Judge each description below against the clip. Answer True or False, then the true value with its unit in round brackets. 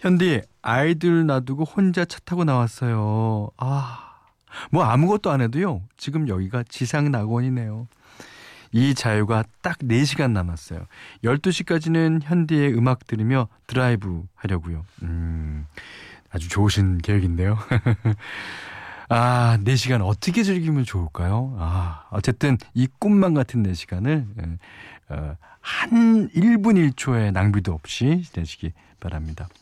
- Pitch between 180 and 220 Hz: False (120 Hz)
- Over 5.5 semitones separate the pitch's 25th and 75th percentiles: True (6.9 semitones)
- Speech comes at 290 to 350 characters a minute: False (250 characters per minute)